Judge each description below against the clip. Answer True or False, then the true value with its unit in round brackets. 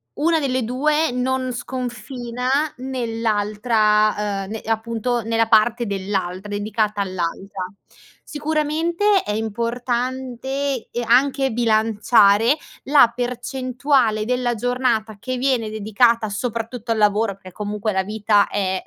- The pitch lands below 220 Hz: False (230 Hz)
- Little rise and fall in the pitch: False (3.2 semitones)